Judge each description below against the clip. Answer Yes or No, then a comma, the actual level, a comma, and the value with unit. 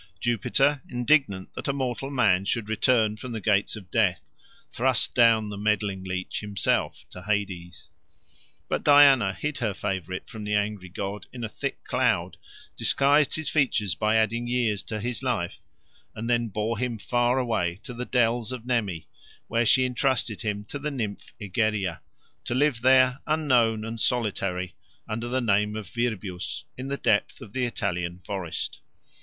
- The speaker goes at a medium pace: Yes, average, 165 wpm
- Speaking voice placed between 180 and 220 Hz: No, low, 110 Hz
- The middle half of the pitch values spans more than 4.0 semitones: No, average, 3.7 semitones